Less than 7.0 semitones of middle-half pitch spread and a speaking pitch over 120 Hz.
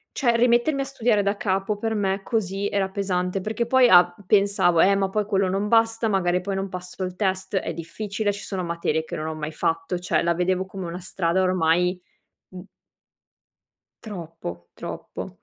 Yes: narrow, 2.6 semitones; high, 190 Hz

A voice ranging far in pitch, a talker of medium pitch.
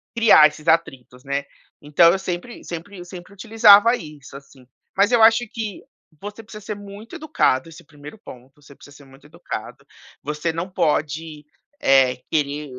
Yes: wide, 5.9 semitones; medium, 165 Hz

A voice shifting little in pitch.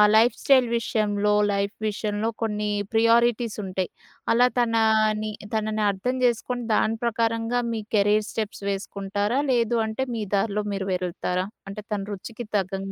Yes: narrow, 2.2 semitones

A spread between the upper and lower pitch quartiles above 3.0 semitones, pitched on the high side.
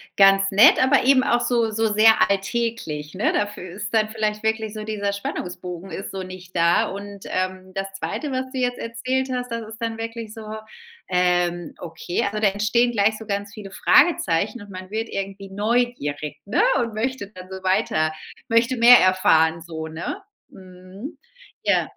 Yes: average, 3.6 semitones; high, 205 Hz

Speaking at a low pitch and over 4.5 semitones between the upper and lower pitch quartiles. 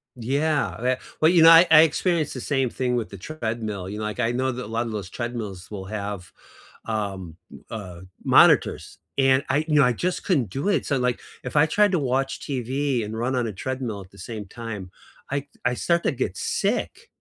Yes: low, 125 Hz; average, 5.1 semitones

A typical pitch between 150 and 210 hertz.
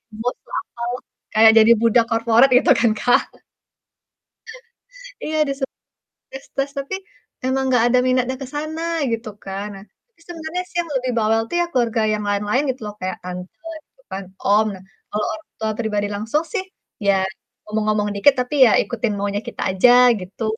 No: high, 230 Hz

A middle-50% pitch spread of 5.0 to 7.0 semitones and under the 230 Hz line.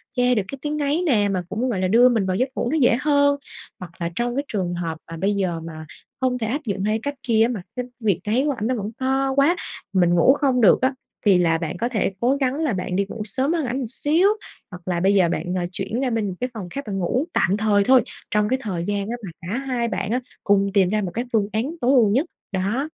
Yes: average, 5.3 semitones; high, 220 Hz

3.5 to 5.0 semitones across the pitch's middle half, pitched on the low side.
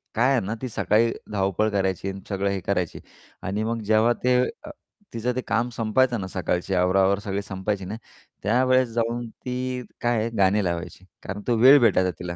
Yes: average, 3.9 semitones; low, 105 Hz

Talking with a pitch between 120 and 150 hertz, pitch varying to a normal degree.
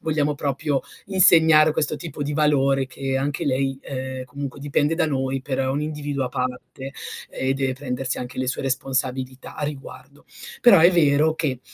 No: medium, 140 Hz; narrow, 2.2 semitones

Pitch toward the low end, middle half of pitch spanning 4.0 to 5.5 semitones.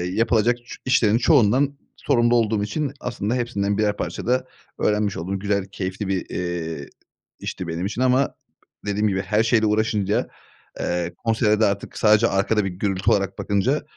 No: low, 105 Hz; average, 3.3 semitones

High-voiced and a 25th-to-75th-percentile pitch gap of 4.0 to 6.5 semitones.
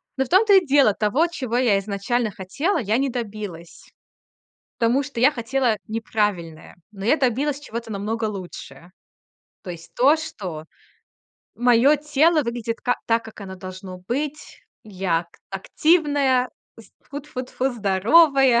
Yes: high, 235 Hz; wide, 5.6 semitones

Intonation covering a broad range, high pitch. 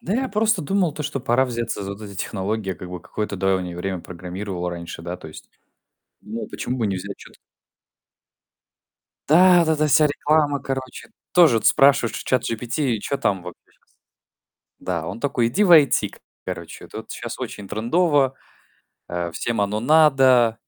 No: wide, 7.2 semitones; low, 115 Hz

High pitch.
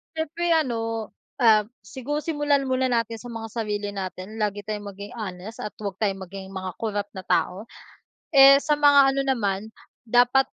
Yes: high, 225 Hz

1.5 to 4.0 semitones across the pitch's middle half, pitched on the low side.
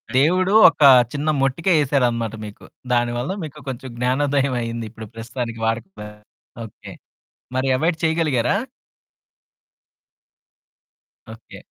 No: average, 4.4 semitones; low, 130 Hz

